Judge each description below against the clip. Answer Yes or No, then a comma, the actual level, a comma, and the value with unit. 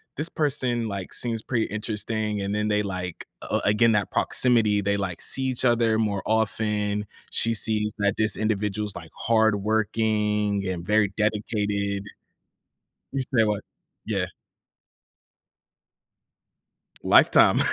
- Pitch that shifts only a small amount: Yes, narrow, 1.6 semitones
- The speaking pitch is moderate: No, low, 105 Hz